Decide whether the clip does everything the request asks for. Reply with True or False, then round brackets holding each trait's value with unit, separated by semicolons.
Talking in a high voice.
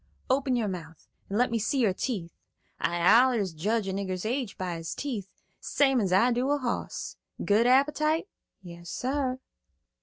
True (230 Hz)